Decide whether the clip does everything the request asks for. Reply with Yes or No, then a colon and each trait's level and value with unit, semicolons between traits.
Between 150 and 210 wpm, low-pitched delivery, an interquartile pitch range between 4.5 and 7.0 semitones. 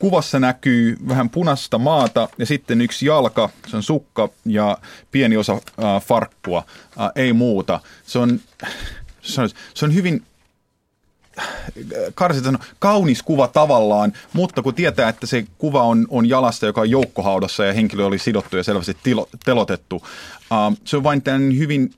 Yes: fast, 155 wpm; low, 125 Hz; average, 4.8 semitones